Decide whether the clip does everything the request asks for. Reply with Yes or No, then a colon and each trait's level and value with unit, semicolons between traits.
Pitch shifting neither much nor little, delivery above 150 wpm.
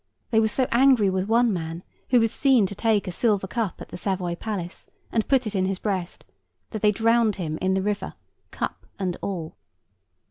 Yes: average, 3.4 semitones; fast, 205 wpm